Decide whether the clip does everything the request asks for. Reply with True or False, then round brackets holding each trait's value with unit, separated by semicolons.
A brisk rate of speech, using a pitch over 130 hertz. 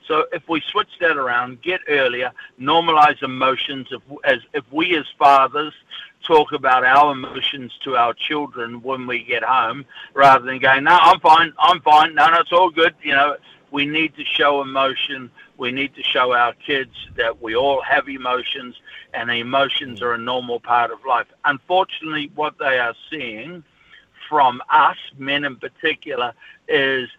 False (170 wpm; 140 Hz)